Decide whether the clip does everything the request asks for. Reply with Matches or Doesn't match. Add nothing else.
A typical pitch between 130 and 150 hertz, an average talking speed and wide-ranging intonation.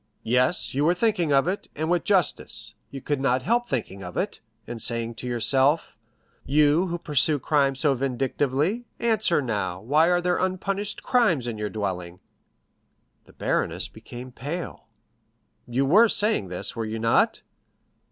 Matches